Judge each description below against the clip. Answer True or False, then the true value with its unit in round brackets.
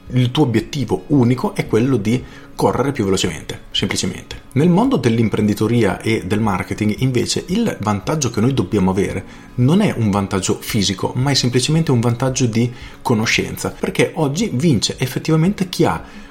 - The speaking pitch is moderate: False (125 Hz)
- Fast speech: False (155 wpm)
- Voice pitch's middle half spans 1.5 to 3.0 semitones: False (5.0 semitones)